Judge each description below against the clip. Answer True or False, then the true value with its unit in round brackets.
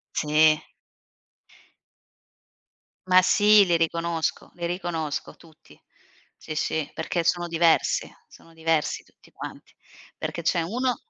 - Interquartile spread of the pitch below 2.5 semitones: True (1.8 semitones)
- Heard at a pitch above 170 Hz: False (165 Hz)